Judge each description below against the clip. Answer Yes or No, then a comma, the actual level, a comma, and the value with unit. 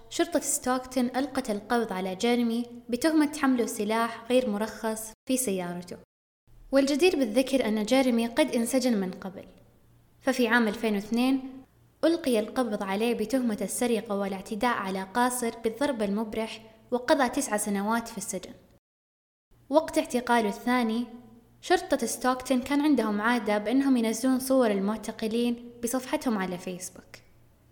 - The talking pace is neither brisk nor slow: Yes, average, 115 wpm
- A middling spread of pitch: Yes, average, 3.3 semitones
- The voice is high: Yes, high, 235 Hz